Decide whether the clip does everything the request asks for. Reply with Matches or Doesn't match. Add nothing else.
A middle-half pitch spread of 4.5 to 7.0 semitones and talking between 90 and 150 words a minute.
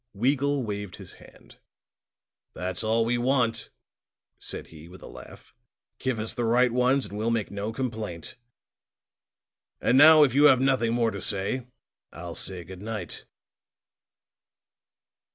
Doesn't match